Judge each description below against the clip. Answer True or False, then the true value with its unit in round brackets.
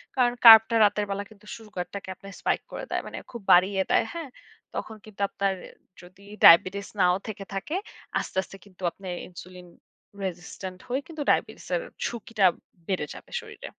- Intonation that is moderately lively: True (3.2 semitones)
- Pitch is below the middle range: False (200 Hz)